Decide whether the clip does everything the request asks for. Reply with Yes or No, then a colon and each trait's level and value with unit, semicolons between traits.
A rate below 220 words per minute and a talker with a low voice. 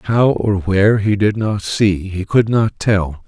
Yes: average, 200 wpm; low, 100 Hz